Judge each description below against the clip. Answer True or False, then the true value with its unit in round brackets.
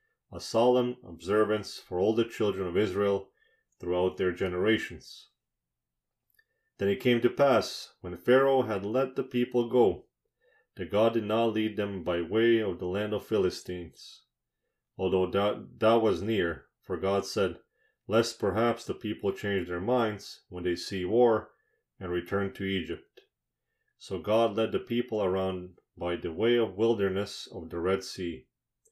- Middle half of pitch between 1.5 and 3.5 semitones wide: False (4.2 semitones)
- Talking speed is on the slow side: False (155 wpm)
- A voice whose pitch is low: True (105 Hz)